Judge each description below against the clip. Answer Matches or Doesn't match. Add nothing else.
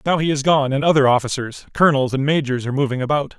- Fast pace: Matches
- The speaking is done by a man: Matches